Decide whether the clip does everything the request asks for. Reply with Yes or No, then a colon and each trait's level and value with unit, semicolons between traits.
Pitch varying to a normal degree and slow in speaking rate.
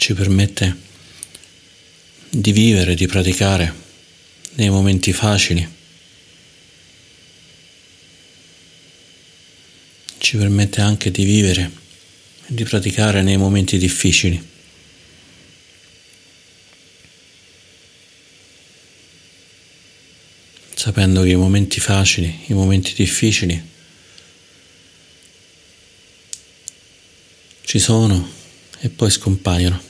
No: narrow, 1.9 semitones; slow, 65 wpm